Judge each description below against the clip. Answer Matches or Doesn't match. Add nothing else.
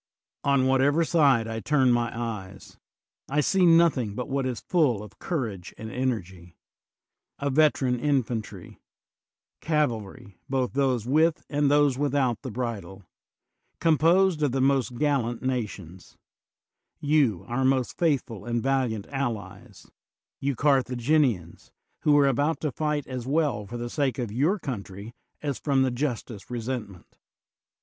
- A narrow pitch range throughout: Doesn't match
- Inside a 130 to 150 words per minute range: Matches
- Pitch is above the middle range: Doesn't match